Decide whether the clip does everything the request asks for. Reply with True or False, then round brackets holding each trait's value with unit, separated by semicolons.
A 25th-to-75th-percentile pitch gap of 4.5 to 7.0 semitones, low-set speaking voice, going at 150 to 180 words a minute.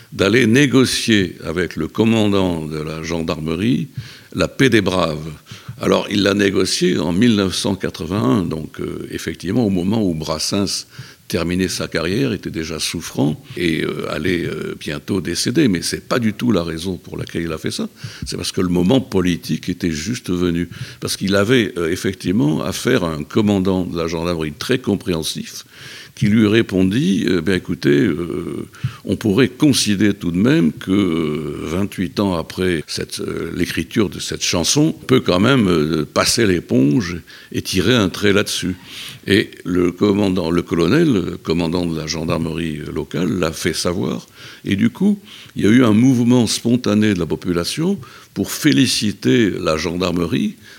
True (5.0 semitones; 95 Hz; 165 wpm)